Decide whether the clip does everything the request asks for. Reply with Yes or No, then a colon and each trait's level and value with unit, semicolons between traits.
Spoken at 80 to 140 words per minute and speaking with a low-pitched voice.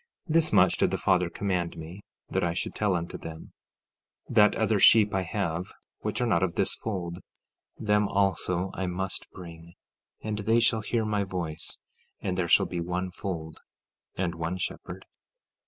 No: average, 175 wpm; very low, 95 Hz